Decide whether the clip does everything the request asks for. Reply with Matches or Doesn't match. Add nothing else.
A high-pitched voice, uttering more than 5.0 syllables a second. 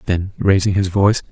Doesn't match